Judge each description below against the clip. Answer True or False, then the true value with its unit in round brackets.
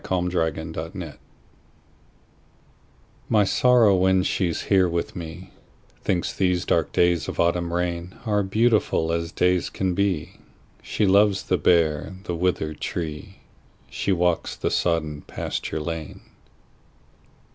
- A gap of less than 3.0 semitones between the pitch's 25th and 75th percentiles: True (2.4 semitones)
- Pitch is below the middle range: True (90 Hz)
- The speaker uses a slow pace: True (110 wpm)